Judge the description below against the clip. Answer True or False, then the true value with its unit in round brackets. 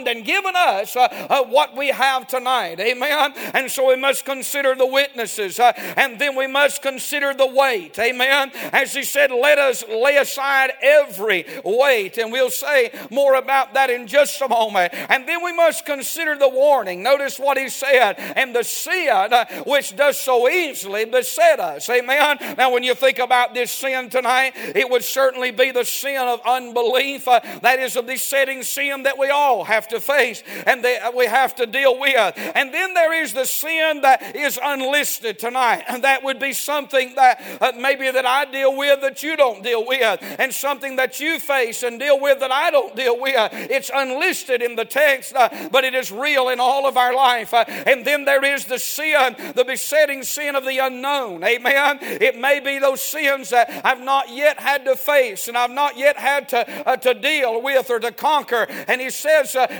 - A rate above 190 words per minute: True (200 wpm)